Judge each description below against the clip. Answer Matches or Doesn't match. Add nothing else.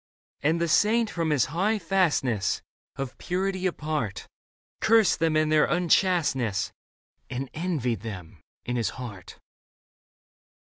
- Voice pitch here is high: Doesn't match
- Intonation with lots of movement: Matches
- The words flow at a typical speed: Doesn't match